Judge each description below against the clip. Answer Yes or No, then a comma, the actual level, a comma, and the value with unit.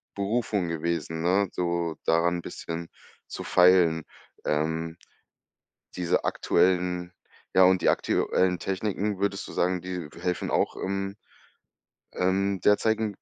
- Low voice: Yes, very low, 90 Hz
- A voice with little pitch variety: Yes, narrow, 2.3 semitones